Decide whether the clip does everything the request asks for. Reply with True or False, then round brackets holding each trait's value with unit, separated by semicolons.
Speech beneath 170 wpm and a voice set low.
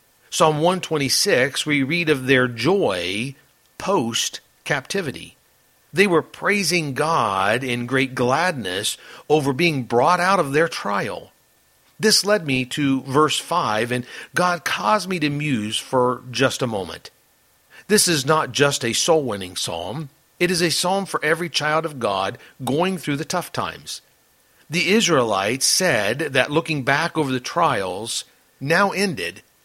False (145 wpm; 150 Hz)